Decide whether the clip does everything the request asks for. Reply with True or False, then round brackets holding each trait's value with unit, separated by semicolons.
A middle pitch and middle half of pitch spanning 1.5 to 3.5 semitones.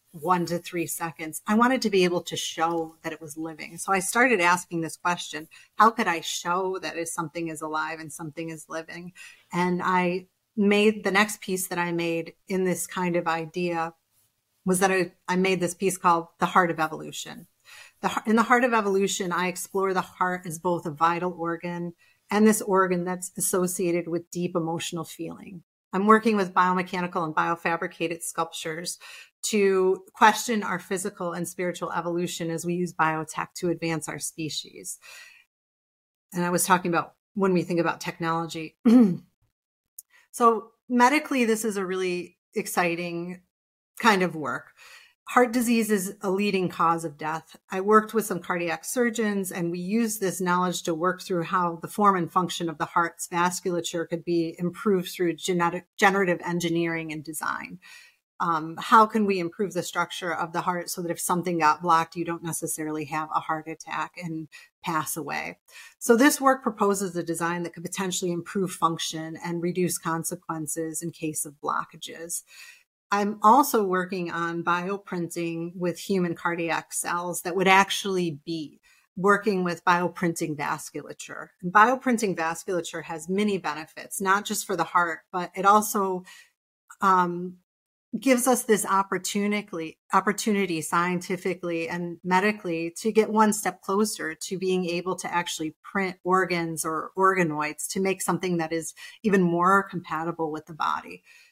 True (175 Hz; 2.8 semitones)